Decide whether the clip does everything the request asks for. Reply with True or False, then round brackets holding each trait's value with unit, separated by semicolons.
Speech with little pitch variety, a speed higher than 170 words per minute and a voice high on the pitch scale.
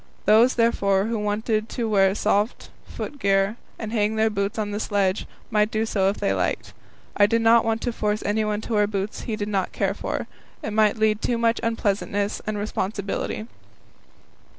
True (1.6 semitones; 190 wpm; 210 Hz)